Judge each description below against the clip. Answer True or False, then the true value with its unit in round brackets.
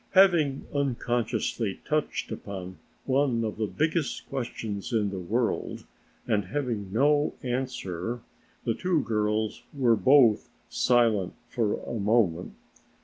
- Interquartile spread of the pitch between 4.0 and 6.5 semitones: True (4.4 semitones)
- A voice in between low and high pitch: False (115 Hz)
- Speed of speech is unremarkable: False (115 wpm)